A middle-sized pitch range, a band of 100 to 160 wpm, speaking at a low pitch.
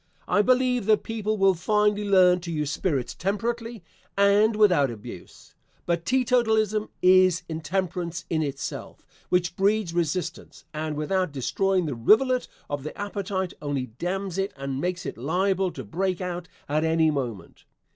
No: average, 4.6 semitones; average, 145 wpm; medium, 185 Hz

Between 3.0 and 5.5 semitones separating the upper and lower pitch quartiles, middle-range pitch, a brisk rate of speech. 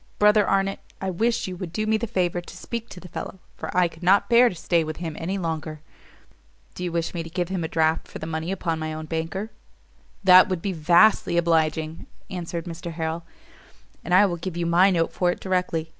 No: narrow, 2.6 semitones; medium, 175 Hz; fast, 225 wpm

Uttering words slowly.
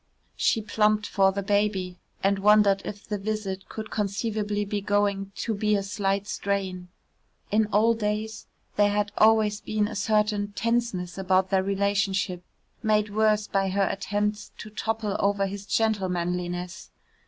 No: average, 145 wpm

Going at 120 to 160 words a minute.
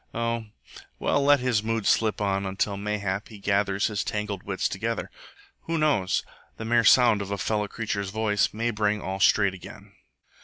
No: average, 175 wpm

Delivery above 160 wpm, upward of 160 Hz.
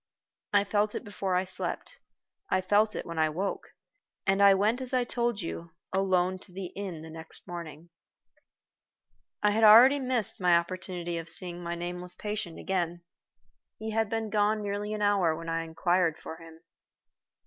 Yes: average, 170 wpm; medium, 185 Hz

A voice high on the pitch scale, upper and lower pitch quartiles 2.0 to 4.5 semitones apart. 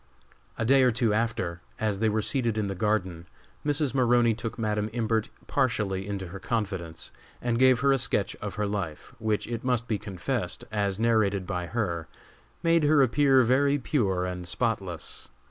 No: low, 110 Hz; average, 4.1 semitones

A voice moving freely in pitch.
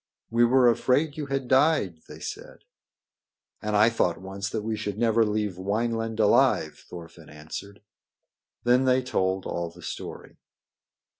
No: average, 4.3 semitones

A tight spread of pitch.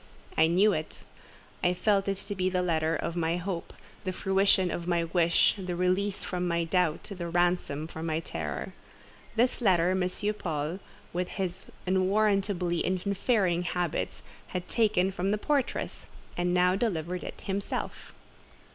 Yes: narrow, 2.3 semitones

